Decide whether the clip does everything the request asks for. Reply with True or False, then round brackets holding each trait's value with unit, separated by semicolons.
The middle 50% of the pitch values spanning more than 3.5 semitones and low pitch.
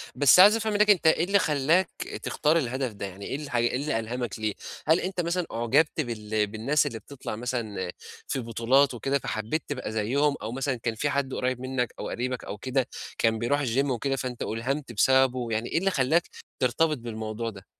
True (4.2 semitones; 130 Hz)